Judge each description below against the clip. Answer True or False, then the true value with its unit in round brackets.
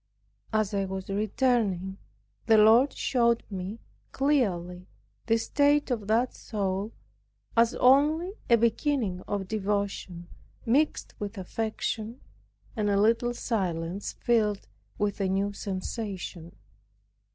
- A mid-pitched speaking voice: False (215 Hz)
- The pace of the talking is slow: True (110 wpm)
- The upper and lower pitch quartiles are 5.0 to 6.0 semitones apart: False (3.4 semitones)